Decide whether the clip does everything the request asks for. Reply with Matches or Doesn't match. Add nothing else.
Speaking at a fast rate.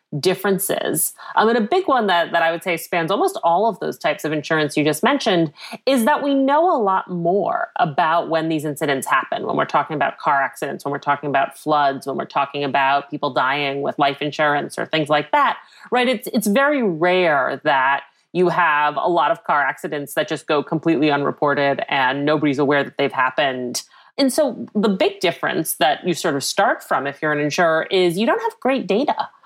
Matches